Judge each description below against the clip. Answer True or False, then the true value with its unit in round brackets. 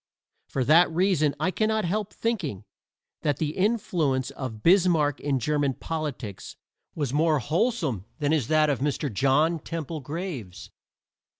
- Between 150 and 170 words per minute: False (135 wpm)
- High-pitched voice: False (155 Hz)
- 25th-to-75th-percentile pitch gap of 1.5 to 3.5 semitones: False (4.0 semitones)